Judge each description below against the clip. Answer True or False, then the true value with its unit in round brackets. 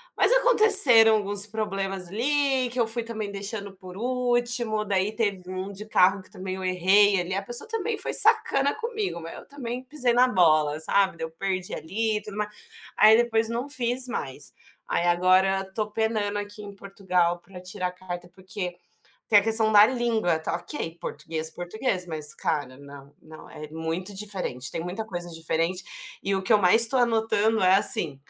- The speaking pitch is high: True (200 Hz)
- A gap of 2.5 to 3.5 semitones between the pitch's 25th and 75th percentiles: False (4.1 semitones)